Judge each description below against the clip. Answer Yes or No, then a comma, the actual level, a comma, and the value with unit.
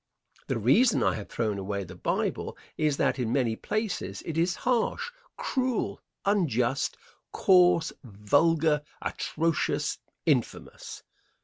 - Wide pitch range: Yes, wide, 8.0 semitones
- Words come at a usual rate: No, slow, 115 wpm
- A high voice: No, medium, 150 Hz